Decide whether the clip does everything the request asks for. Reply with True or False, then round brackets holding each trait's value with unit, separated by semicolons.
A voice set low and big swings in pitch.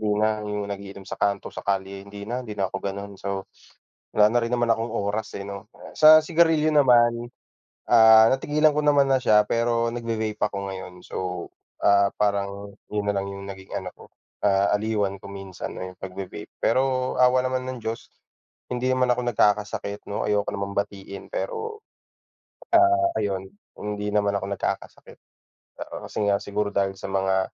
False (105 Hz; 3.3 semitones)